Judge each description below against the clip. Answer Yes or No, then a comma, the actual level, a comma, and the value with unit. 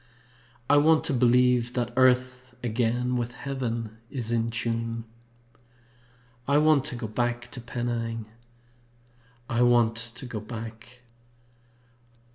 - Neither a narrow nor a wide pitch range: No, narrow, 1.5 semitones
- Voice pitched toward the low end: Yes, low, 120 Hz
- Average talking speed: No, slow, 115 wpm